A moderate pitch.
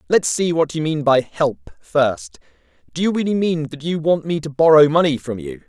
Yes: medium, 145 Hz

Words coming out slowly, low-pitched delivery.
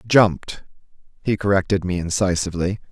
Yes: slow, 105 wpm; very low, 95 Hz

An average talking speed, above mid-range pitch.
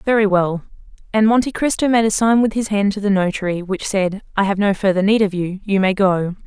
No: fast, 240 wpm; high, 200 Hz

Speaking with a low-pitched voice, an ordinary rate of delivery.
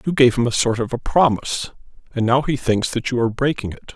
No: low, 125 Hz; fast, 260 wpm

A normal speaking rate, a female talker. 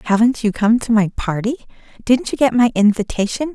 Yes: average, 185 wpm; female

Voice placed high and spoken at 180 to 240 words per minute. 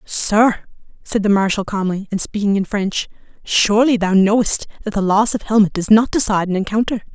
Yes: high, 205 Hz; average, 185 wpm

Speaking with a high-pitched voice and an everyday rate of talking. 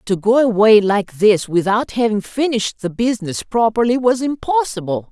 Yes: high, 220 Hz; average, 150 wpm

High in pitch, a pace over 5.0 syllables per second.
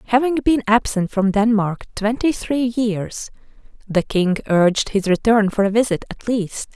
No: high, 215 Hz; 4.4 syllables/s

